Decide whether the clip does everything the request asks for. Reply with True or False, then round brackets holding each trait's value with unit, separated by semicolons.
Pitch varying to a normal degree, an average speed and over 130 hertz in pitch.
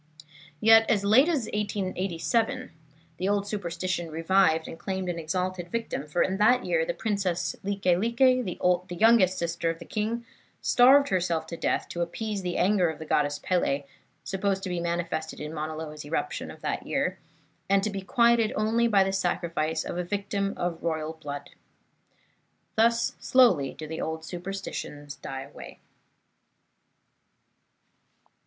True (4.3 semitones; 155 wpm; 185 Hz)